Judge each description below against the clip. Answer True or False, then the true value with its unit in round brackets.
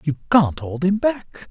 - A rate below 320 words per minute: True (200 wpm)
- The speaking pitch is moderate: True (175 Hz)